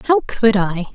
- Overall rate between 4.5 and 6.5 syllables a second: No, 4.2 syllables/s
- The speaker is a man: No, female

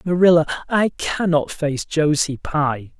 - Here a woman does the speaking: No, male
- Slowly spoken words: Yes, slow, 120 wpm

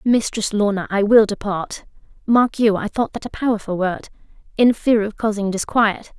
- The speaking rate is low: No, average, 155 wpm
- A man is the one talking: No, female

